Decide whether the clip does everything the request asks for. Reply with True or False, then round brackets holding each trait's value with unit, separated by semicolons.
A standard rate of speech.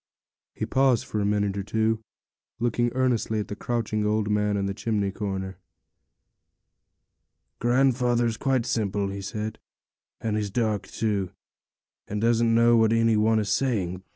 True (150 wpm)